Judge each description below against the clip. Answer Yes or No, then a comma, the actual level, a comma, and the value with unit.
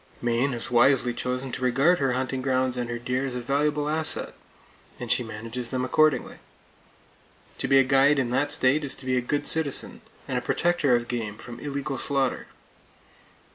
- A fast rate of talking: No, average, 185 wpm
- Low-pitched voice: Yes, low, 130 Hz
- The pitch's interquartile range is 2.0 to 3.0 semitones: Yes, narrow, 2.5 semitones